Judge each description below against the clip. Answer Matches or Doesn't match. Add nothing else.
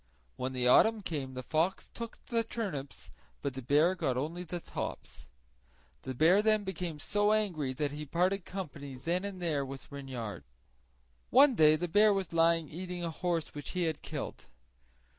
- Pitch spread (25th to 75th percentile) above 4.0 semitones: Matches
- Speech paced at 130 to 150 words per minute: Doesn't match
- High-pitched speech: Doesn't match